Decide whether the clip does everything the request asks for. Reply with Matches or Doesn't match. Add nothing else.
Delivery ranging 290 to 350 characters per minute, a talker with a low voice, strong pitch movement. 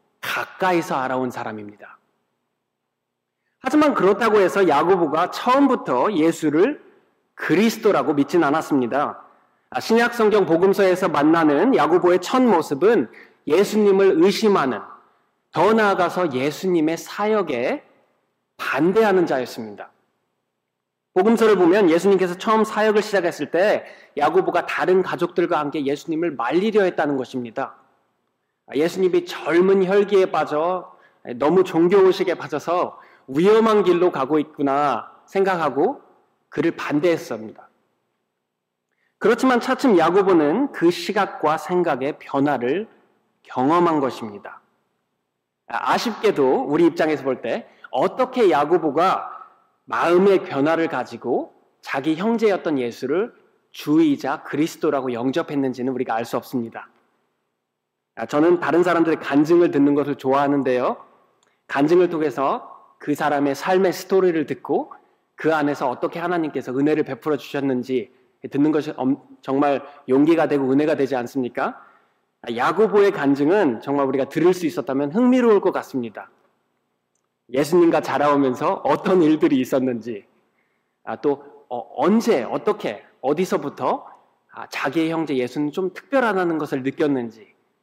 Doesn't match